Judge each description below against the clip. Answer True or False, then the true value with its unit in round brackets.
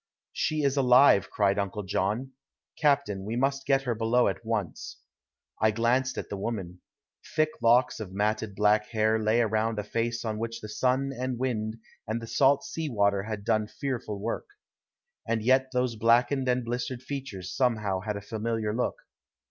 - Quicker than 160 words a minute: True (170 wpm)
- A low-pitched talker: True (115 Hz)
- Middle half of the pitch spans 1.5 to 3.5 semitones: True (3.2 semitones)